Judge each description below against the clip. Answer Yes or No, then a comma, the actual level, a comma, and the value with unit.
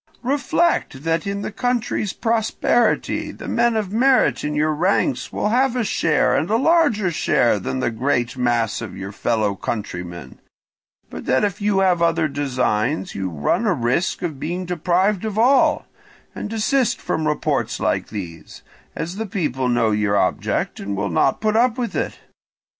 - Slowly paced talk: No, average, 170 wpm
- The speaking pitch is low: No, medium, 170 Hz